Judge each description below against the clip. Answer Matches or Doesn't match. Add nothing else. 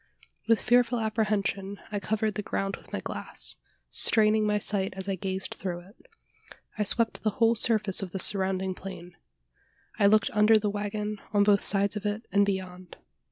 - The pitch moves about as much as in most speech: Doesn't match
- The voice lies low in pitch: Doesn't match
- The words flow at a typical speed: Matches